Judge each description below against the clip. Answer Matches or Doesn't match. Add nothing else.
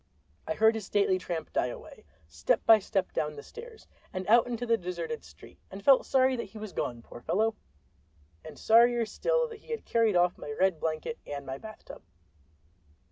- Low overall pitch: Doesn't match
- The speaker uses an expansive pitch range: Matches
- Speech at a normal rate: Matches